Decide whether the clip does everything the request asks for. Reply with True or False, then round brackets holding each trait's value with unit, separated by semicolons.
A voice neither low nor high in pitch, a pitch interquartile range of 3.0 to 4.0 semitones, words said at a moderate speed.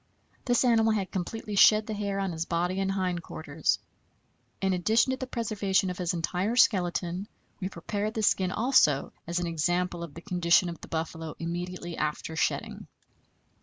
True (180 Hz; 3.6 semitones; 170 wpm)